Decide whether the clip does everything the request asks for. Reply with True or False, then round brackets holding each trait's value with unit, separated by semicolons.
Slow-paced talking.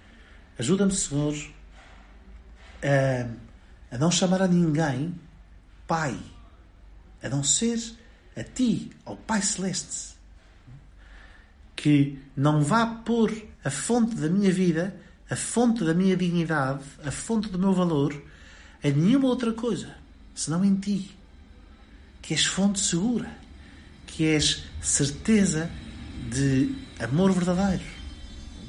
True (110 wpm)